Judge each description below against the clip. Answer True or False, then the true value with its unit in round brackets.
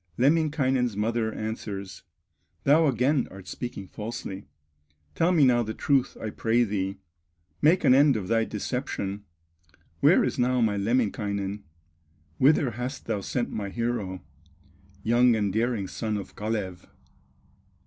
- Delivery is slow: True (130 wpm)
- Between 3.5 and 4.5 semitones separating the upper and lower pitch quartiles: True (3.9 semitones)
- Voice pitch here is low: True (115 Hz)